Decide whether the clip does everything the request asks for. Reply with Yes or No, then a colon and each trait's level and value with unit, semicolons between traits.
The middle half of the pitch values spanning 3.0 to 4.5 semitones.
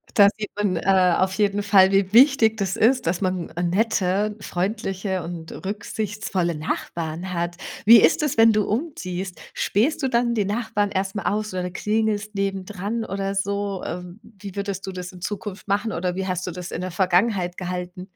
No: narrow, 2.6 semitones